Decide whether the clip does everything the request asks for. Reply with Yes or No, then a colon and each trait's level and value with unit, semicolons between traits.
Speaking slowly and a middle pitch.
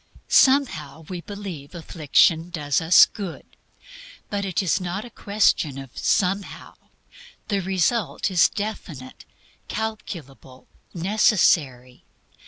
Yes: slow, 100 wpm; medium, 180 Hz